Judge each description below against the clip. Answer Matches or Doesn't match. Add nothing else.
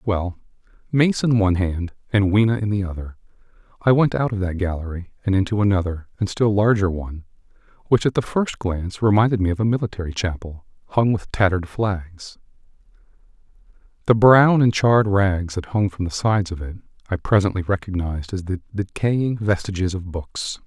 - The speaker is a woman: Doesn't match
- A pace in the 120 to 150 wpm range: Doesn't match